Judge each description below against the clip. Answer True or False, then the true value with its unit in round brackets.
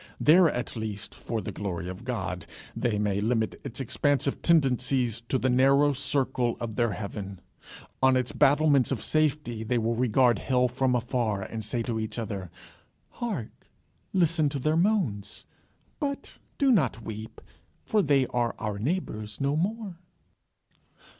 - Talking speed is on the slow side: False (150 wpm)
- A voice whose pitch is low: True (125 Hz)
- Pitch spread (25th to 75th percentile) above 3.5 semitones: True (4.7 semitones)